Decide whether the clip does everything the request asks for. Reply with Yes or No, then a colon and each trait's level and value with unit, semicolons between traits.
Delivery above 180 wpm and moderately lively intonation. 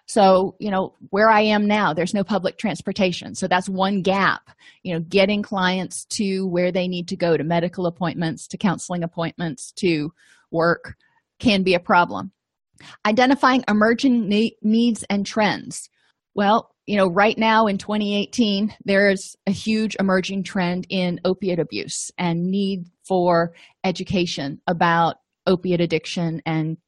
No: average, 150 wpm; average, 3.1 semitones